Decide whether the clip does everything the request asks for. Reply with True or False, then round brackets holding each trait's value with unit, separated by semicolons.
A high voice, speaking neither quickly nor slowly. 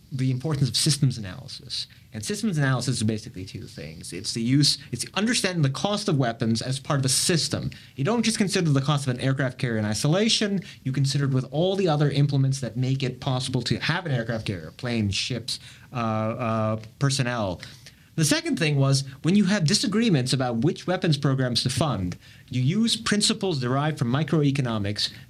False (135 Hz; 190 wpm)